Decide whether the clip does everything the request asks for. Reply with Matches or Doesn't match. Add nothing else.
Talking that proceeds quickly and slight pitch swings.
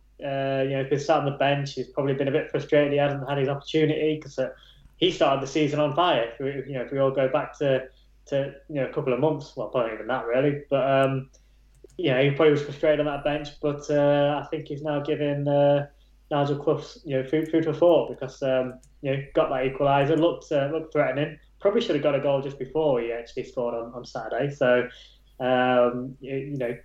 Matches